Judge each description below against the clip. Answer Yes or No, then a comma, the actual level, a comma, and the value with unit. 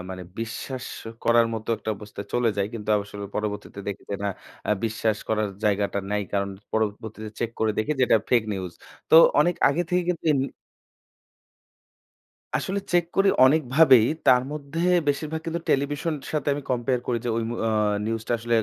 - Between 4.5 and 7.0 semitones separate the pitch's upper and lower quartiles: Yes, average, 5.2 semitones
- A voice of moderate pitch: No, low, 115 Hz